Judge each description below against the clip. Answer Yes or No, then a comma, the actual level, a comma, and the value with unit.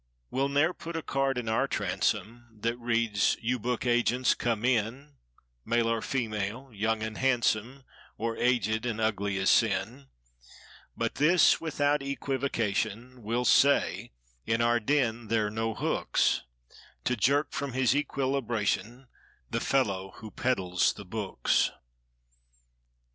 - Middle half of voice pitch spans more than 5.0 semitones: No, average, 3.4 semitones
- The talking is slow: Yes, slow, 120 wpm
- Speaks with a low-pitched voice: Yes, low, 120 Hz